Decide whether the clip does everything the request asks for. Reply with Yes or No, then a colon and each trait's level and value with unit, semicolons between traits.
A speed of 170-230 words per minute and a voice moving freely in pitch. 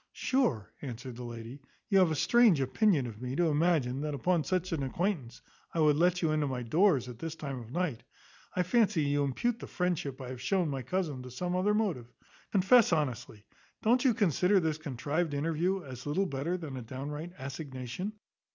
Yes: average, 195 wpm; wide, 5.7 semitones